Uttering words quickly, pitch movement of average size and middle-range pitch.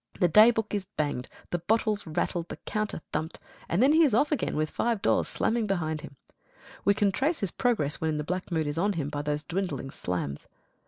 No: fast, 210 wpm; wide, 5.9 semitones; medium, 180 Hz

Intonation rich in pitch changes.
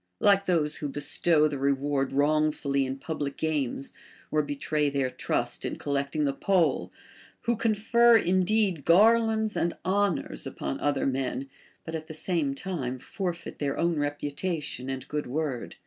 No: average, 4.6 semitones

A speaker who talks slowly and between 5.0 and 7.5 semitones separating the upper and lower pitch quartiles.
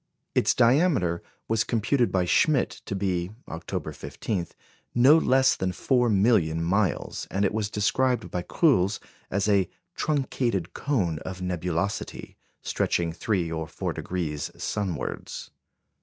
Yes: slow, 125 wpm; wide, 5.5 semitones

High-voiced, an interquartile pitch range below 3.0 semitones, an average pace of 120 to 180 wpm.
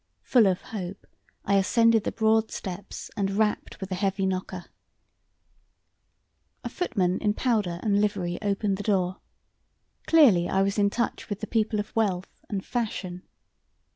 Yes: high, 200 Hz; narrow, 2.6 semitones; average, 150 wpm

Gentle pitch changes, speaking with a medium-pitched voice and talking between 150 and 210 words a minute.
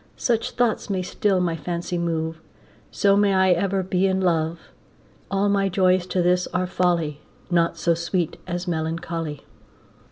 Yes: narrow, 2.2 semitones; medium, 180 Hz; average, 155 wpm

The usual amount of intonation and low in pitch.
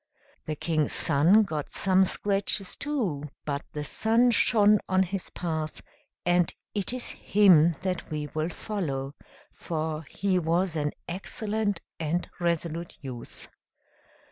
No: average, 4.5 semitones; medium, 175 Hz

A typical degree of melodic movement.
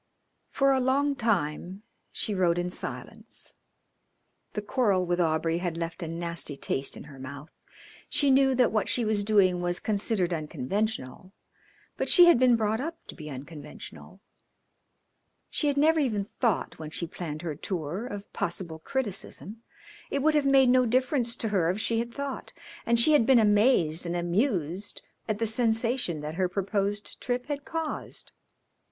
No: wide, 6.6 semitones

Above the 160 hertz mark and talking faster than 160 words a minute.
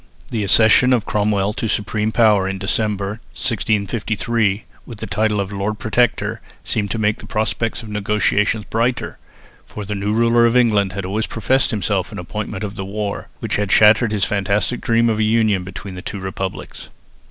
No: low, 105 Hz; average, 185 wpm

